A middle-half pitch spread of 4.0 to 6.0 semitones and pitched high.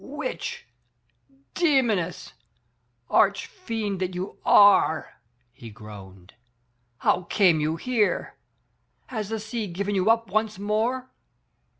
Yes: average, 4.4 semitones; high, 205 Hz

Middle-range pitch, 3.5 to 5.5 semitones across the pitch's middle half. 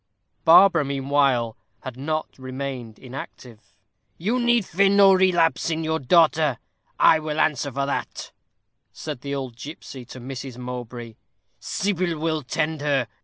Yes: medium, 145 Hz; average, 4.1 semitones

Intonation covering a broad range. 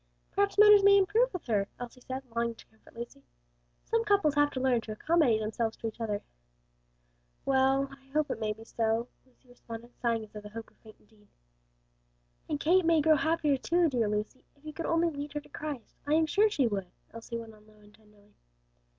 Yes: wide, 6.0 semitones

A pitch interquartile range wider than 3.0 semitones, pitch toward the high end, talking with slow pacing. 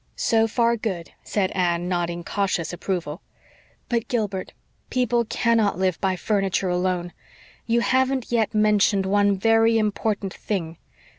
Yes: average, 3.6 semitones; high, 200 Hz; slow, 130 wpm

